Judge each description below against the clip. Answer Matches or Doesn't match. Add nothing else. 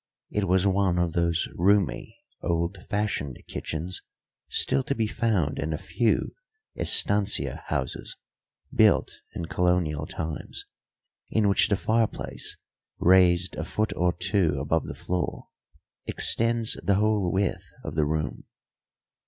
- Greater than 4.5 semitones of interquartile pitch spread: Doesn't match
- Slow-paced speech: Matches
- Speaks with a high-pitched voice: Doesn't match